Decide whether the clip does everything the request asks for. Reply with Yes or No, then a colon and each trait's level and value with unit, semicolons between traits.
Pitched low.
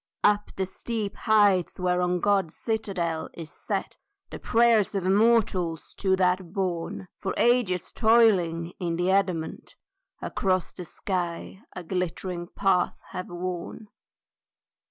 No: medium, 185 Hz